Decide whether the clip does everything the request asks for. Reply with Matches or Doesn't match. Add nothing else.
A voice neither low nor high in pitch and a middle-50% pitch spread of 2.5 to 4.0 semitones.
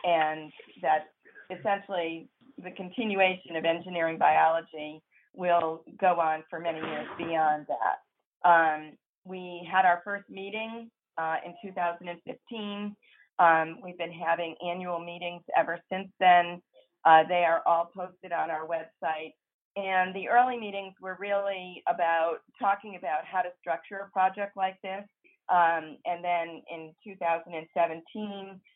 Matches